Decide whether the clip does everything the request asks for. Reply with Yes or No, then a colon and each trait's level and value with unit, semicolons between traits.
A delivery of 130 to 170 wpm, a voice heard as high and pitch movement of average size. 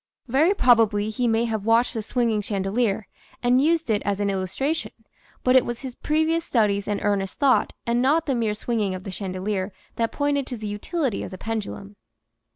No: average, 190 wpm; high, 225 Hz; average, 4.0 semitones